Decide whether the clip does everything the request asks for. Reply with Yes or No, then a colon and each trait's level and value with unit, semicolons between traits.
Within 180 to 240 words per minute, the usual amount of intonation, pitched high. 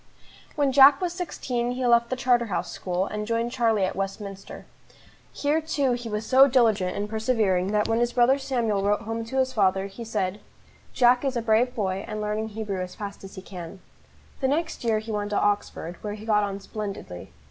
Yes: average, 200 wpm; average, 3.6 semitones; high, 220 Hz